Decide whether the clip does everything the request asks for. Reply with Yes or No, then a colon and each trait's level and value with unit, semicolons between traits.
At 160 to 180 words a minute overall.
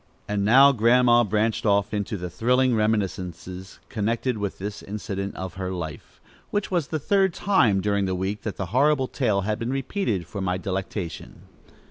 Yes: average, 170 wpm